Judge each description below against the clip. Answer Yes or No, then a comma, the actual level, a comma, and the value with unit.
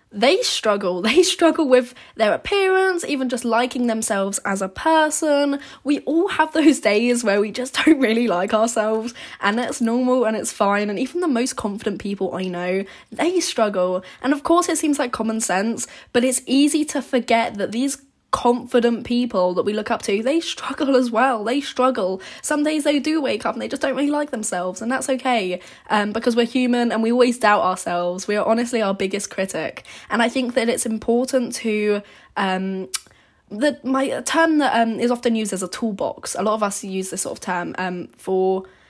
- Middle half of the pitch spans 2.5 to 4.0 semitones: No, average, 4.7 semitones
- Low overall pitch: No, high, 240 Hz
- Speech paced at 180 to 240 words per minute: Yes, average, 200 wpm